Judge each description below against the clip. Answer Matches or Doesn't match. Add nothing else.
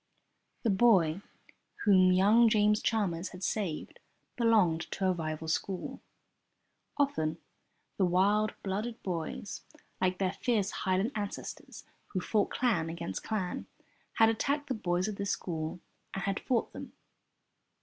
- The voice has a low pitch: Doesn't match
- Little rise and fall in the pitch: Doesn't match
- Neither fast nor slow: Doesn't match